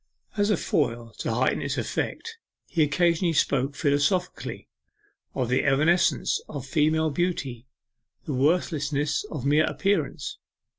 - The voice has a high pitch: No, medium, 150 Hz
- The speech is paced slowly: Yes, slow, 120 wpm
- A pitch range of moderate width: Yes, average, 3.9 semitones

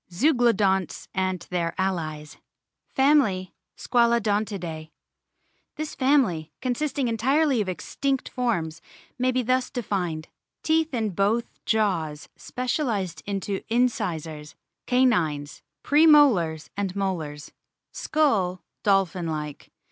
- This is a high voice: Yes, high, 200 Hz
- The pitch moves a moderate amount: No, wide, 6.9 semitones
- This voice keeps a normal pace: No, slow, 95 wpm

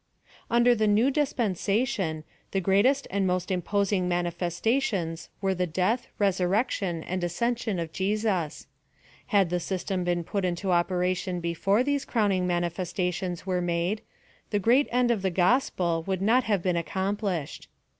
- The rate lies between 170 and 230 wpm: No, average, 145 wpm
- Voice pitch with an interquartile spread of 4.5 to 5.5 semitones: No, average, 3.3 semitones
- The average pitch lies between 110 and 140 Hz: No, high, 190 Hz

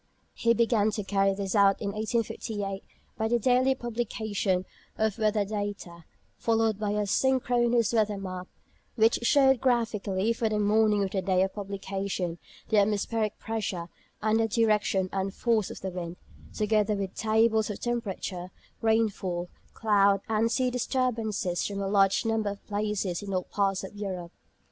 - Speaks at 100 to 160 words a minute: Yes, average, 155 wpm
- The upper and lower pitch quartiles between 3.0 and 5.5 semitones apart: No, narrow, 2.4 semitones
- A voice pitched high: Yes, high, 210 Hz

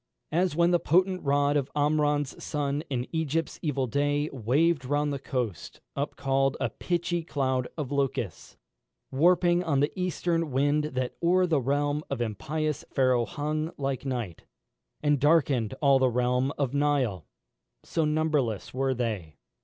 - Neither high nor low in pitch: Yes, medium, 145 Hz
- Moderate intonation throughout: Yes, average, 3.0 semitones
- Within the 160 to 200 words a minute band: No, average, 150 wpm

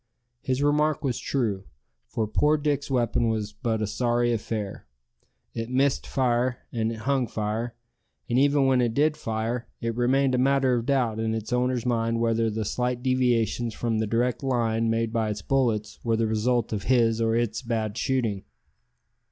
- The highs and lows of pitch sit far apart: No, narrow, 2.4 semitones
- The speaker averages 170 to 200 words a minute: Yes, average, 175 wpm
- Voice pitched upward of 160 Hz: No, low, 120 Hz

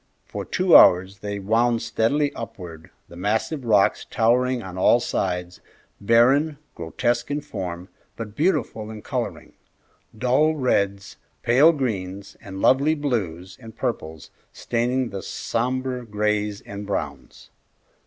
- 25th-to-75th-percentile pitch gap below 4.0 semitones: No, average, 4.6 semitones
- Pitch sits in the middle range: No, low, 115 Hz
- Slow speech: Yes, slow, 125 wpm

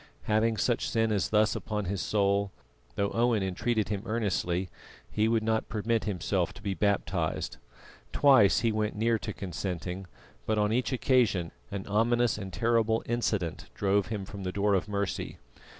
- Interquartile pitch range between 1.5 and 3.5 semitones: Yes, narrow, 2.4 semitones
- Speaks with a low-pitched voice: Yes, low, 105 Hz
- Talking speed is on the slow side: No, average, 165 wpm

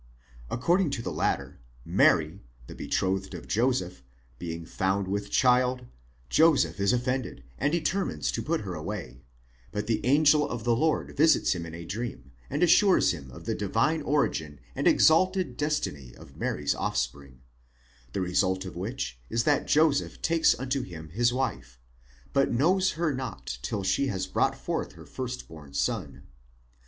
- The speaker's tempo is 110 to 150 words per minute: No, average, 160 wpm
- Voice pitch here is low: Yes, low, 115 Hz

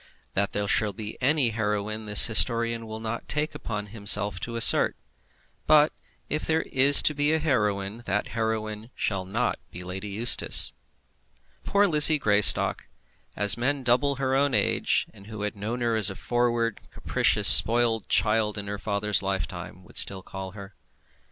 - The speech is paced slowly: No, average, 160 wpm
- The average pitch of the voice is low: Yes, low, 110 Hz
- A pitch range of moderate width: Yes, average, 3.1 semitones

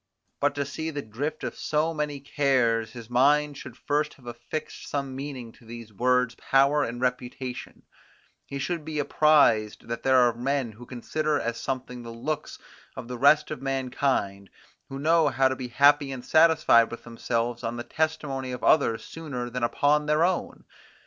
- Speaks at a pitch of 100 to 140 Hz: Yes, low, 135 Hz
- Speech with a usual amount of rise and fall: Yes, average, 3.7 semitones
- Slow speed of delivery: No, average, 175 wpm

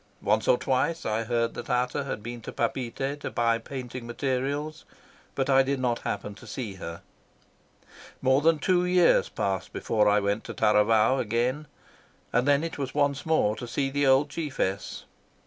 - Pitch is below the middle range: Yes, low, 125 Hz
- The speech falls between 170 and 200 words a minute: Yes, average, 175 wpm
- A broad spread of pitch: No, average, 3.8 semitones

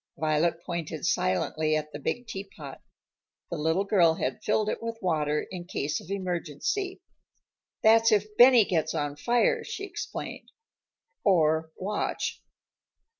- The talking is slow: Yes, slow, 130 wpm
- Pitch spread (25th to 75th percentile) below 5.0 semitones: No, wide, 5.6 semitones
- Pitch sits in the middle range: Yes, medium, 175 Hz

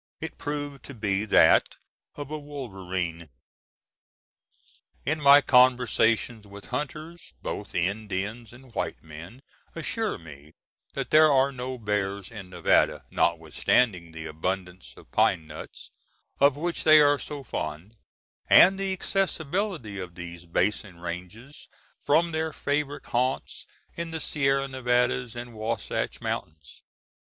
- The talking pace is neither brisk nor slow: No, slow, 125 wpm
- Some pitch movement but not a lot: No, wide, 7.7 semitones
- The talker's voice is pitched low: Yes, low, 120 Hz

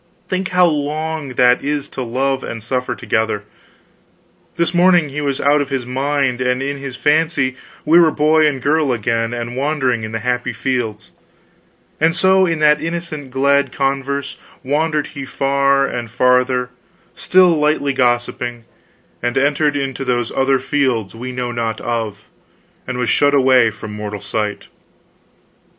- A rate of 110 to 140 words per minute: No, average, 155 wpm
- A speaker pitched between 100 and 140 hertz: Yes, low, 135 Hz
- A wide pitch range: No, average, 3.3 semitones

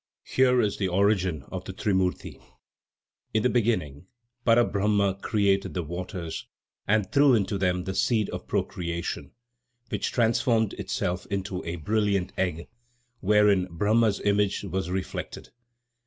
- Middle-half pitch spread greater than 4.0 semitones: No, average, 2.8 semitones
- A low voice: Yes, low, 100 Hz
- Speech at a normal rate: No, slow, 130 wpm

